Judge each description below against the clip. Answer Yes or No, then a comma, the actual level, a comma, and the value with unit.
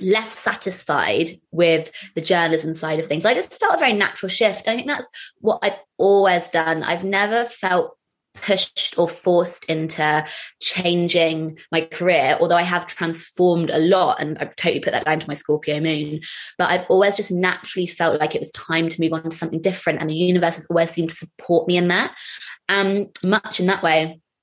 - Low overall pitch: No, medium, 170 Hz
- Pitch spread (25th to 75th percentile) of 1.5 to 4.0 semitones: Yes, average, 2.9 semitones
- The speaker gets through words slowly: No, average, 195 wpm